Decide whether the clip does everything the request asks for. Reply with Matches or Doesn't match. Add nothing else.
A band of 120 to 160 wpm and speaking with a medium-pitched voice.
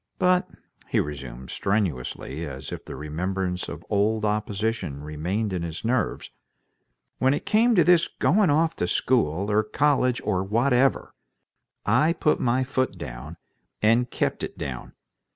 Doesn't match